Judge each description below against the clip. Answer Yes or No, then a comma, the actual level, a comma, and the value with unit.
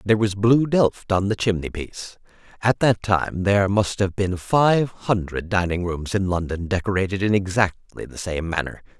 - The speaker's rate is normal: Yes, average, 180 wpm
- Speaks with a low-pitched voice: Yes, low, 100 Hz